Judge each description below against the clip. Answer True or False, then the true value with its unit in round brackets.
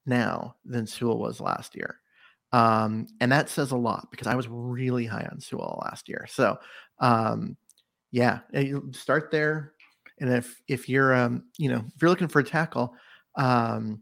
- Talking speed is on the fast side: False (175 wpm)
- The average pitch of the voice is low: True (125 Hz)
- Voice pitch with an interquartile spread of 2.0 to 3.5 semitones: True (2.9 semitones)